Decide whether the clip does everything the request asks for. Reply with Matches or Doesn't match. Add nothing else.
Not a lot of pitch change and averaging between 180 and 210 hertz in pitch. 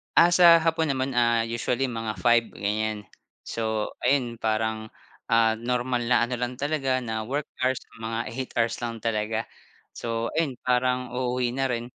Doesn't match